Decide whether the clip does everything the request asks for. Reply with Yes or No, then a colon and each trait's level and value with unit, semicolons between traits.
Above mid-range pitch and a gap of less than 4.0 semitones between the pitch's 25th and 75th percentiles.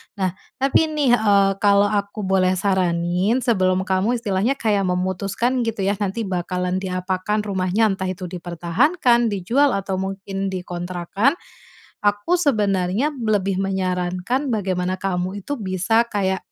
Yes: high, 195 Hz; average, 3.0 semitones